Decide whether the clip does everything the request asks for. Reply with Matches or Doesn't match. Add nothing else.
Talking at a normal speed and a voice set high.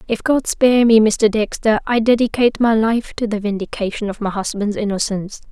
Matches